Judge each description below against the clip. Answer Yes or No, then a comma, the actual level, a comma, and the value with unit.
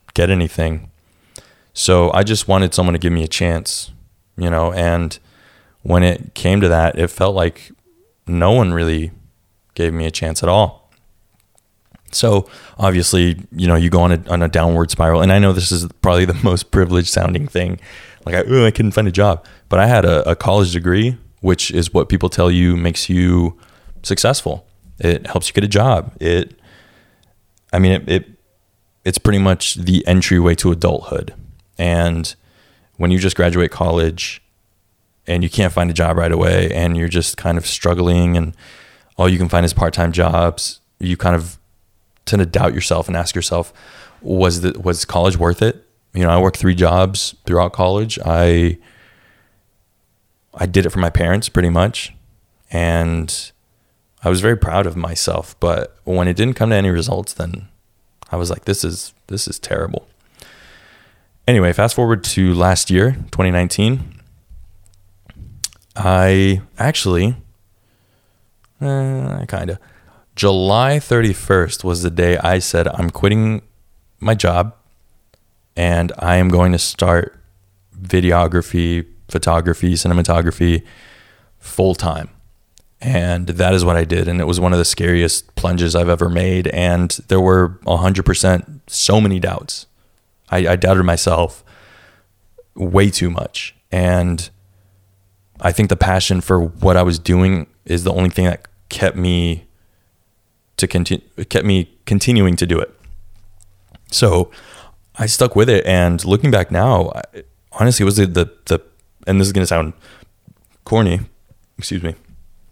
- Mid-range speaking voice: No, very low, 90 Hz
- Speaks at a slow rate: No, average, 160 wpm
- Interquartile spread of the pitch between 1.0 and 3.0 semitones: Yes, narrow, 2.4 semitones